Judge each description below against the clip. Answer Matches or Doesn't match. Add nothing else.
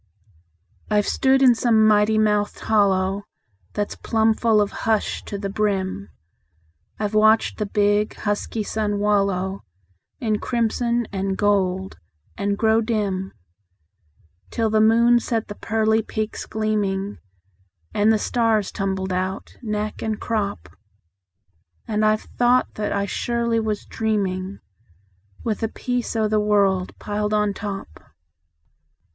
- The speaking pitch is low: Doesn't match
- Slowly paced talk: Matches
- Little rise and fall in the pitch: Matches